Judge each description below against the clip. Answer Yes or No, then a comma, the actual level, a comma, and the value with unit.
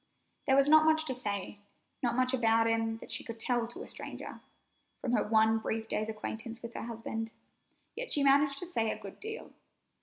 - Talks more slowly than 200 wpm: No, fast, 205 wpm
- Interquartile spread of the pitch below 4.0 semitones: Yes, average, 3.5 semitones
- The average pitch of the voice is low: No, high, 230 Hz